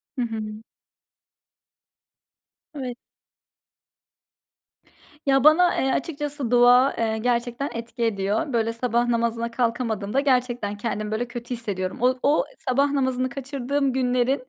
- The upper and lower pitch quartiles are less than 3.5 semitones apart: Yes, average, 2.7 semitones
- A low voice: No, high, 245 Hz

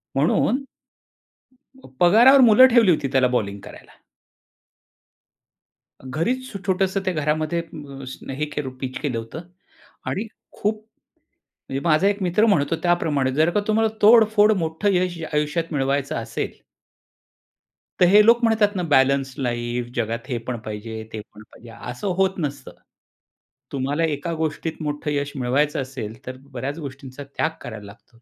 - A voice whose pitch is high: No, medium, 150 Hz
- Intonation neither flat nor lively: No, wide, 6.4 semitones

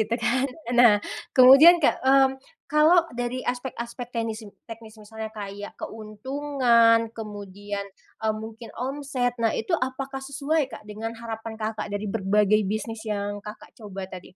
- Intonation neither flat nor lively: Yes, average, 3.6 semitones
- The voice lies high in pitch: Yes, high, 225 Hz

